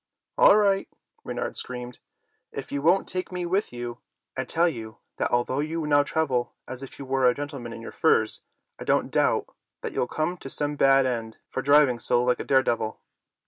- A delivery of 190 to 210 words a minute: Yes, average, 195 wpm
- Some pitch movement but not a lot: Yes, average, 4.1 semitones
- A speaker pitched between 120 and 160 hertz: Yes, low, 135 Hz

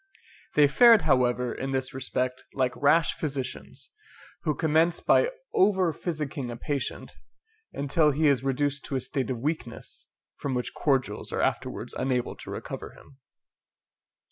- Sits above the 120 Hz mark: Yes, medium, 140 Hz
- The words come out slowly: No, average, 145 wpm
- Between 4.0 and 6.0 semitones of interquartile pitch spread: No, average, 3.2 semitones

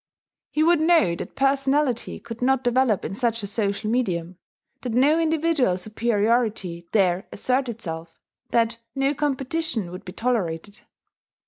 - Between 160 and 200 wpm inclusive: No, slow, 135 wpm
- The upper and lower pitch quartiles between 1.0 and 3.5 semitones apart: No, wide, 5.4 semitones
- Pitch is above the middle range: Yes, high, 235 Hz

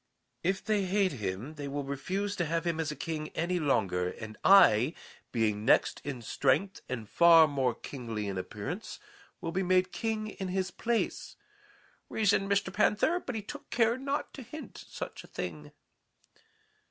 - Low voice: No, medium, 170 Hz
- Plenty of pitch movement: Yes, wide, 8.0 semitones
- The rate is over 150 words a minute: Yes, average, 165 wpm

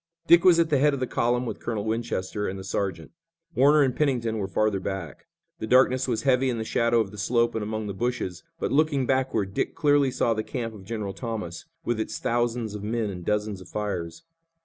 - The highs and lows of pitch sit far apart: No, average, 3.8 semitones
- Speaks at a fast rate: Yes, fast, 220 wpm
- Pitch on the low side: Yes, low, 115 Hz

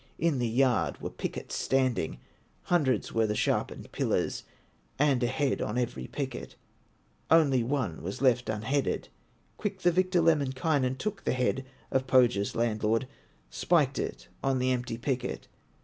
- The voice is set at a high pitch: No, low, 130 Hz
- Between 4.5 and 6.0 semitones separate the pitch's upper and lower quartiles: No, average, 3.5 semitones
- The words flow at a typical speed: Yes, average, 150 wpm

